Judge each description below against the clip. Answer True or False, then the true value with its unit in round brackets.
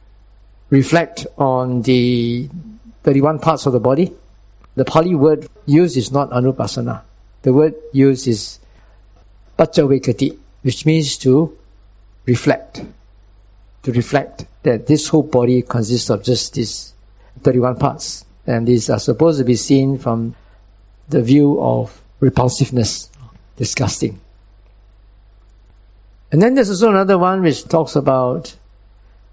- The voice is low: True (125 Hz)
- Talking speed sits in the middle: False (120 wpm)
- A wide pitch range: True (5.9 semitones)